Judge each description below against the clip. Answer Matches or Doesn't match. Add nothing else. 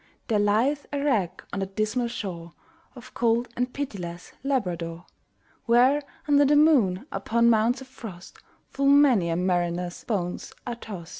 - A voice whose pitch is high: Matches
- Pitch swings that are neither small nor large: Doesn't match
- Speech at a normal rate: Matches